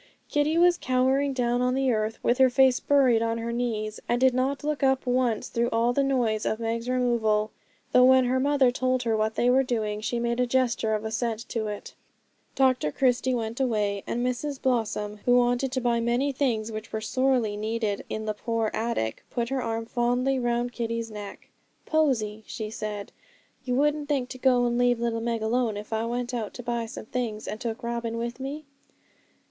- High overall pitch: Yes, high, 240 Hz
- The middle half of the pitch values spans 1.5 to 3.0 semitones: Yes, narrow, 2.5 semitones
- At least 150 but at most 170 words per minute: No, average, 200 wpm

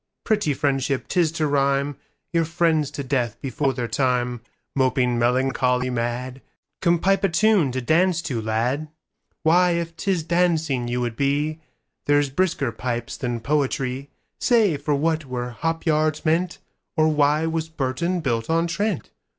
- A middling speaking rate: No, slow, 130 wpm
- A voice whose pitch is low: No, medium, 145 Hz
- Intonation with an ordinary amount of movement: Yes, average, 4.5 semitones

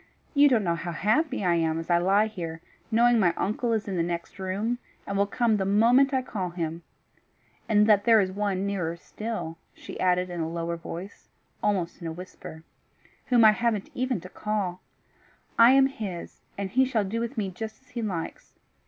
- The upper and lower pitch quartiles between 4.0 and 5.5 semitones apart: Yes, average, 4.6 semitones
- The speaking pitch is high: Yes, high, 200 Hz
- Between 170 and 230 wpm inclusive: Yes, average, 200 wpm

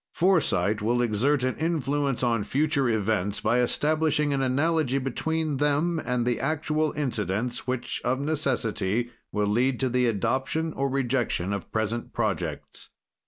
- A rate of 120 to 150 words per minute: Yes, average, 140 wpm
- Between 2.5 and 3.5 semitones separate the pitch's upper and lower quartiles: No, average, 4.2 semitones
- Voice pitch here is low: Yes, low, 130 Hz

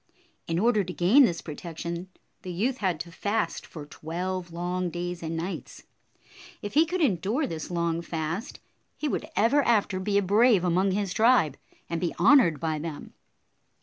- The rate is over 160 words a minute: Yes, average, 170 wpm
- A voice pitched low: No, medium, 180 Hz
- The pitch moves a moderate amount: Yes, average, 4.1 semitones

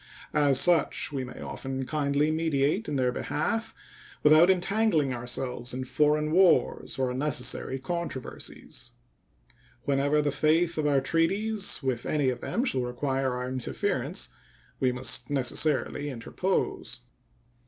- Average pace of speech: No, slow, 125 wpm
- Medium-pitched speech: Yes, medium, 145 Hz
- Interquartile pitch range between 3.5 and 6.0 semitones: Yes, average, 3.8 semitones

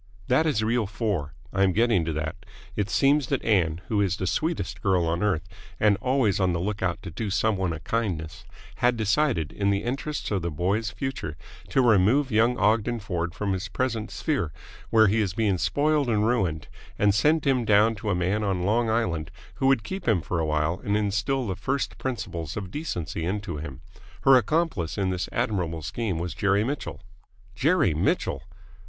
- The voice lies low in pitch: Yes, low, 105 Hz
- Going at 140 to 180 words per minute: No, average, 190 wpm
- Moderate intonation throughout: Yes, average, 5.0 semitones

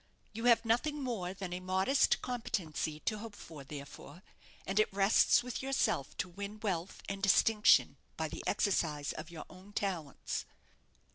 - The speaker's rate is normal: Yes, average, 155 wpm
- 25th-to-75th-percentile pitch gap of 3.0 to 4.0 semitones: No, average, 4.6 semitones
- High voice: Yes, high, 195 Hz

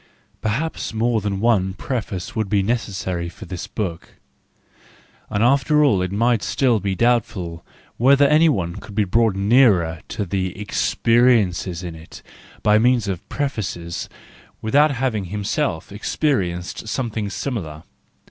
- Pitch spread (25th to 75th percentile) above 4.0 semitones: Yes, average, 4.7 semitones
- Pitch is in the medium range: No, low, 105 Hz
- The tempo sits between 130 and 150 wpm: Yes, slow, 135 wpm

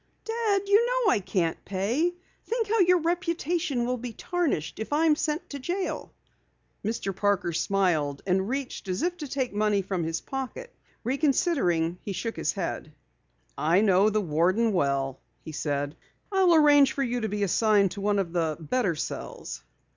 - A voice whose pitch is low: No, high, 220 Hz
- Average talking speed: Yes, average, 170 wpm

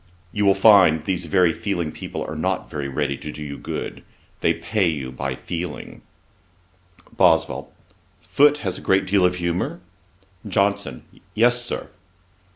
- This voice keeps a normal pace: Yes, average, 150 wpm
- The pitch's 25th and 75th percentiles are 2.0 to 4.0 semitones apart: No, average, 4.7 semitones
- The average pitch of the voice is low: Yes, very low, 90 Hz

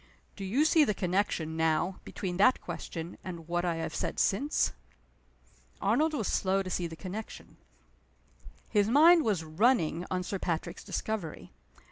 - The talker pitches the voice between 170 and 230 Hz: Yes, medium, 185 Hz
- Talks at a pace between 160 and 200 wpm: No, average, 150 wpm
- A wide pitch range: No, average, 4.5 semitones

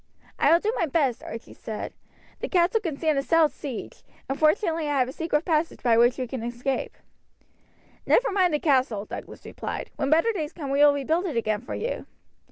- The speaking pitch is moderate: No, very high, 295 Hz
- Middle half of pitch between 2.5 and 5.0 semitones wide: Yes, average, 4.4 semitones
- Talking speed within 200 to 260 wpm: Yes, fast, 205 wpm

